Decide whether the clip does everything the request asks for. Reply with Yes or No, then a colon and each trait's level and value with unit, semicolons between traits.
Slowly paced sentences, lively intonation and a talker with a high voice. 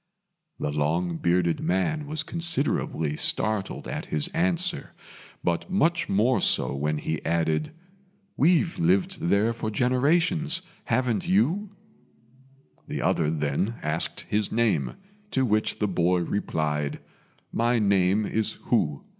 No: slow, 120 wpm; wide, 8.4 semitones; low, 105 Hz